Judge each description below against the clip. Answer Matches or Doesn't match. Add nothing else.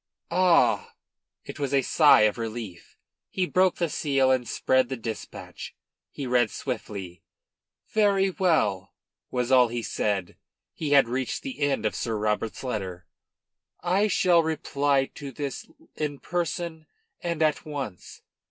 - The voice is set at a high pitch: Doesn't match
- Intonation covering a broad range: Matches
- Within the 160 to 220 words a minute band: Doesn't match